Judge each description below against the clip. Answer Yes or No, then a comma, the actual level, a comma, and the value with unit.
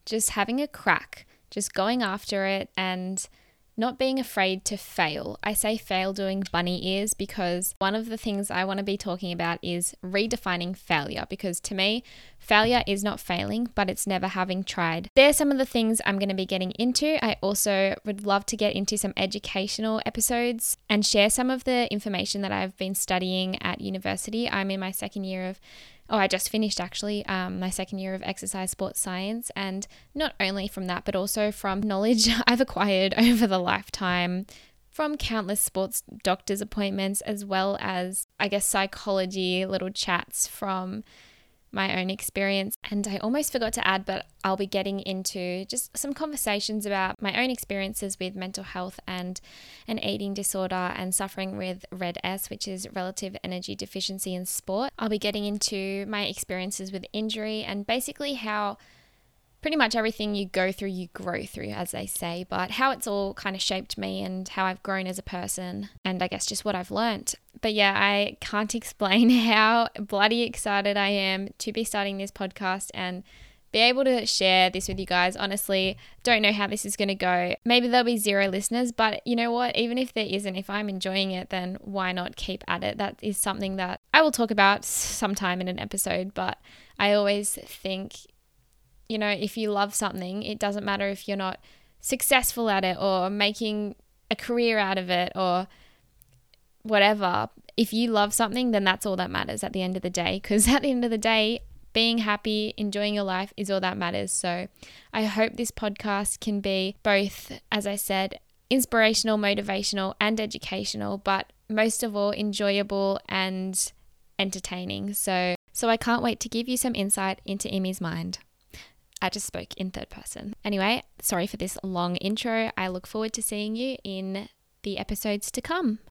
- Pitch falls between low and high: No, high, 200 Hz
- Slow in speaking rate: No, average, 190 wpm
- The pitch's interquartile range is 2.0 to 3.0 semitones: Yes, narrow, 2.5 semitones